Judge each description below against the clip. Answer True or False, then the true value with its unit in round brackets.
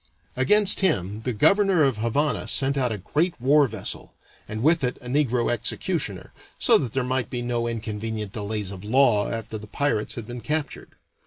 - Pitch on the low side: True (120 Hz)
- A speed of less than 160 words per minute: False (180 wpm)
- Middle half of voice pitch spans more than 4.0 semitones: True (4.5 semitones)